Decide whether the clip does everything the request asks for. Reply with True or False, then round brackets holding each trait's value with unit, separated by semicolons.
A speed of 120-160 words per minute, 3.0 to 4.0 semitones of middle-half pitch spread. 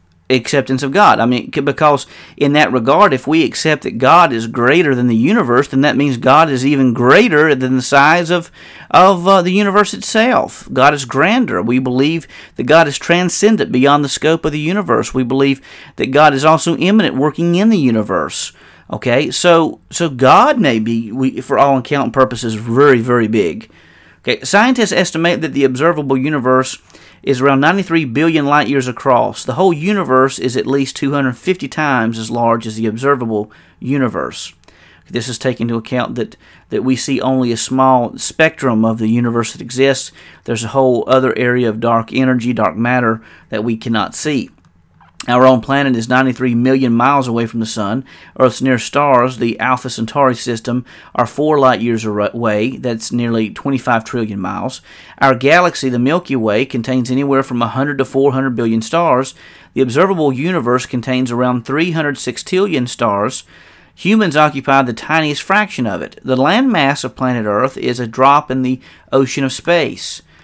False (175 wpm; 3.6 semitones)